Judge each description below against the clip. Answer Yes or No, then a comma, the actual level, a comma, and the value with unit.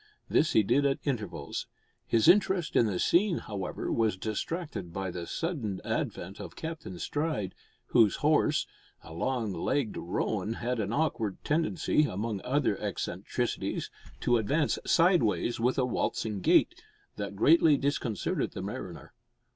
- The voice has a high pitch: No, low, 115 Hz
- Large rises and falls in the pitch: Yes, wide, 7.0 semitones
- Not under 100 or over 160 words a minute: Yes, average, 140 wpm